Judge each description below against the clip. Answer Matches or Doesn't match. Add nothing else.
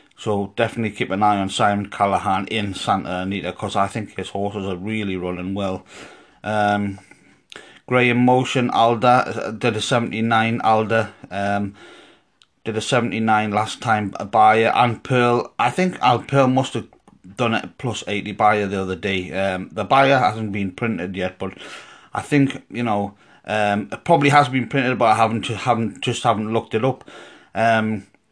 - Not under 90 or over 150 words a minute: Doesn't match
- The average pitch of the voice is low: Matches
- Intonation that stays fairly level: Doesn't match